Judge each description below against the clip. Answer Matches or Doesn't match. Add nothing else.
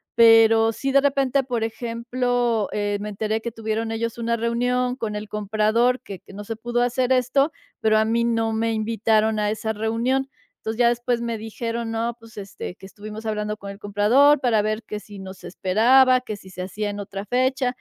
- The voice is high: Matches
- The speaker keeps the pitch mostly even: Matches